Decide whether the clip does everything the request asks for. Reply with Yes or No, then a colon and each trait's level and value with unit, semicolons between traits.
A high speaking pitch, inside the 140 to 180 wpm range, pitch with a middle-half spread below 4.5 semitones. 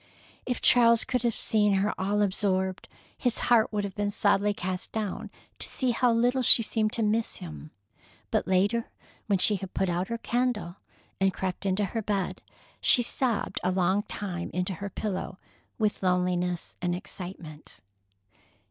Yes: high, 200 Hz; average, 165 wpm; average, 3.4 semitones